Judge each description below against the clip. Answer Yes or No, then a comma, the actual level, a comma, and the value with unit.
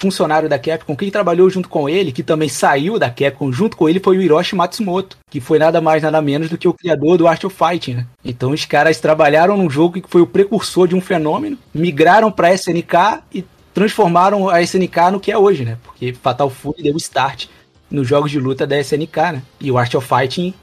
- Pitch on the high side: No, medium, 165 Hz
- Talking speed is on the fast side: Yes, fast, 225 wpm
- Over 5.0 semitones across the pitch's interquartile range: No, average, 3.9 semitones